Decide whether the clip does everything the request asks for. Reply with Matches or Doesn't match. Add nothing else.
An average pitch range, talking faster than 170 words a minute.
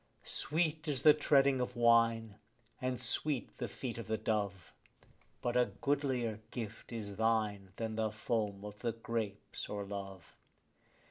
Doesn't match